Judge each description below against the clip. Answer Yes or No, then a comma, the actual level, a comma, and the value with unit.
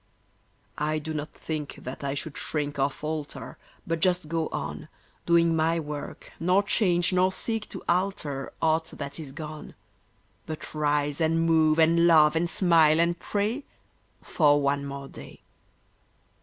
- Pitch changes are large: No, narrow, 2.4 semitones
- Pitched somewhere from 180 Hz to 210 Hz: No, medium, 160 Hz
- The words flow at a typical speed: Yes, average, 150 wpm